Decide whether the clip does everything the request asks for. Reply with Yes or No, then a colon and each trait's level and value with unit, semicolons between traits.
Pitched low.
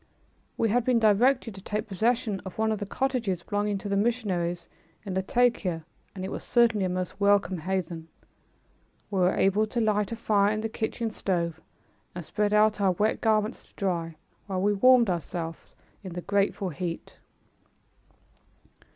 No: high, 200 Hz